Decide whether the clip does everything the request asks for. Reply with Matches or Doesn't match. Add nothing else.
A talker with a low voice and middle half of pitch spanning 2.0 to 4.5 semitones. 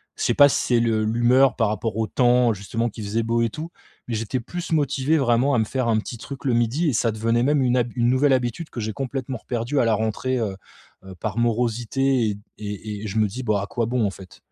Matches